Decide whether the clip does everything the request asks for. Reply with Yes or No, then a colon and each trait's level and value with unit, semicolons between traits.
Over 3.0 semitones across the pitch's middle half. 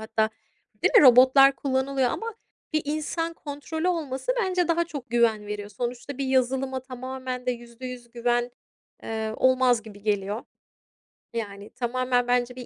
No: narrow, 2.5 semitones